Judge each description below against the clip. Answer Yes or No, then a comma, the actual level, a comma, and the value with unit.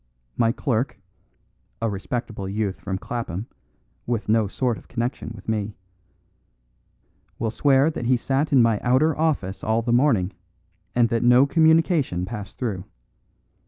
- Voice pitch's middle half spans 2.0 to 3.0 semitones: No, average, 3.9 semitones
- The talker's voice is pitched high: No, low, 115 Hz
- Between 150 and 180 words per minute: No, average, 140 wpm